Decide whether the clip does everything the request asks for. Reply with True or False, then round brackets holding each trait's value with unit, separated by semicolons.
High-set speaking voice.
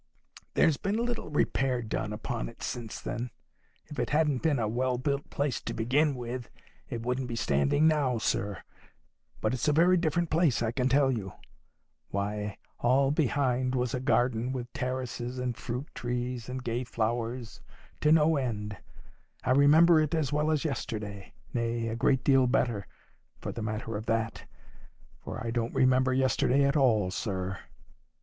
False (125 Hz)